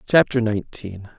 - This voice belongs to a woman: No, male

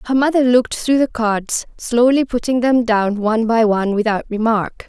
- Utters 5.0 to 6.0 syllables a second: Yes, 5.1 syllables/s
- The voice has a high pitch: Yes, high, 230 Hz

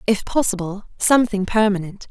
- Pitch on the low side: No, high, 205 Hz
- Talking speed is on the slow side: Yes, slow, 115 wpm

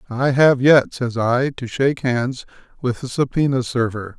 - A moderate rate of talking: Yes, average, 170 wpm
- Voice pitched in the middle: No, low, 130 Hz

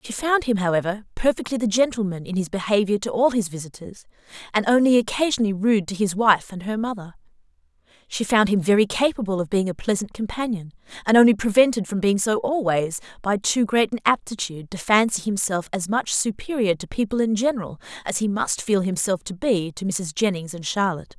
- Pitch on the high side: Yes, high, 205 Hz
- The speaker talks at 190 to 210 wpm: Yes, average, 195 wpm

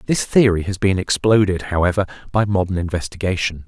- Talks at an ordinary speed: Yes, average, 145 wpm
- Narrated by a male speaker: Yes, male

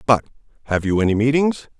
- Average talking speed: Yes, average, 165 wpm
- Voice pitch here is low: Yes, low, 125 Hz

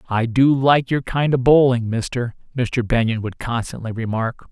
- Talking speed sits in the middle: Yes, average, 175 wpm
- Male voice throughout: Yes, male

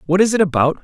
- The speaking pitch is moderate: Yes, medium, 175 Hz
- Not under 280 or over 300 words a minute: Yes, fast, 285 wpm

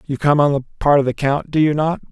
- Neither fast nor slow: No, fast, 310 wpm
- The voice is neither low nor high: Yes, medium, 145 Hz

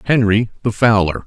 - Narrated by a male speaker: Yes, male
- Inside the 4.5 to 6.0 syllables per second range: Yes, 5.4 syllables/s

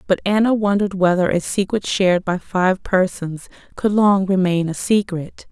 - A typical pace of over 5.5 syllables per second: No, 4.7 syllables/s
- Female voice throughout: Yes, female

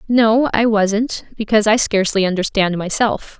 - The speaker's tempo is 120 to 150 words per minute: Yes, average, 140 wpm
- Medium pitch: No, high, 210 Hz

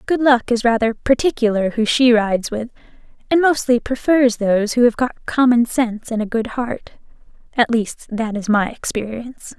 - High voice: Yes, high, 235 Hz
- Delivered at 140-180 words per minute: Yes, average, 175 wpm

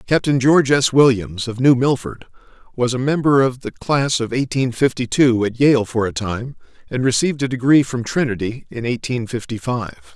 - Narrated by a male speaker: Yes, male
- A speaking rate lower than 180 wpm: No, average, 190 wpm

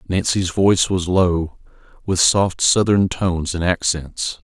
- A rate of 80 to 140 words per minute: Yes, slow, 135 wpm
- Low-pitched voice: Yes, very low, 90 Hz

